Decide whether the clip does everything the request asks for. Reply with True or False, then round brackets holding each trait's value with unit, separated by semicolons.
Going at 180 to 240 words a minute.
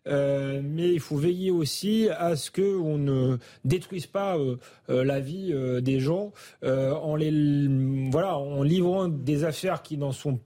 True (185 wpm)